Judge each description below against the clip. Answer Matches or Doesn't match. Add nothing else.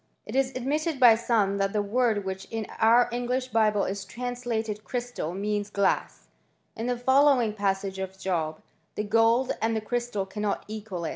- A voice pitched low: Doesn't match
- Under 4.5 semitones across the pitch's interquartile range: Matches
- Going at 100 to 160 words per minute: Doesn't match